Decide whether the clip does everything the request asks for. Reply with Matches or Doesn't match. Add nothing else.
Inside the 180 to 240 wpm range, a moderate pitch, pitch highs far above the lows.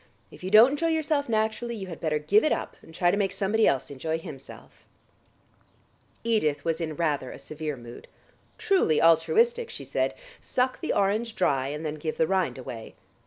Matches